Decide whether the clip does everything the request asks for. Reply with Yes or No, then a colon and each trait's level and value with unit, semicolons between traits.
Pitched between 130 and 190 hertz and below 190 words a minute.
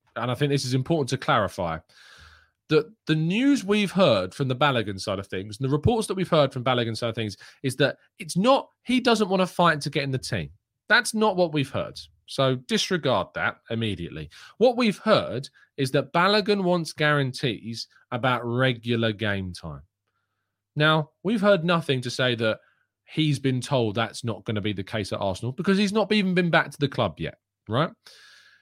No: medium, 140 Hz; average, 200 wpm